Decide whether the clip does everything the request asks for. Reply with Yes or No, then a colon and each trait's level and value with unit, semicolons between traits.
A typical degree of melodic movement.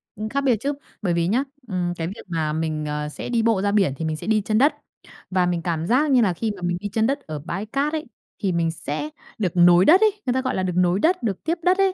No: wide, 6.9 semitones